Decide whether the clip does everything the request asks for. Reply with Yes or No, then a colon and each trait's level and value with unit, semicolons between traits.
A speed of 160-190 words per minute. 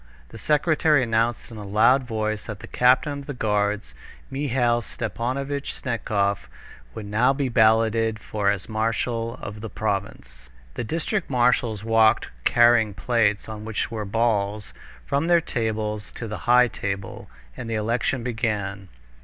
No: average, 145 wpm